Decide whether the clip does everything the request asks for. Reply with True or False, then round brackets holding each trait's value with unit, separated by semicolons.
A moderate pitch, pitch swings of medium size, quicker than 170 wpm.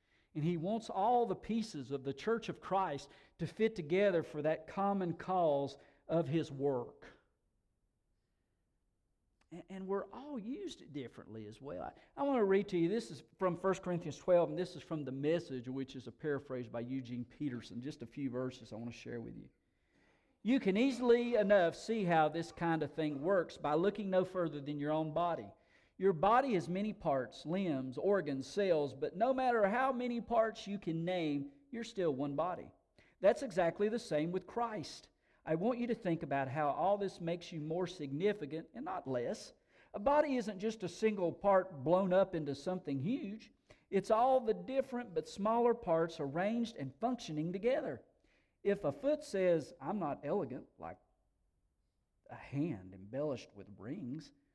False (170 Hz; 6.5 semitones; 180 wpm)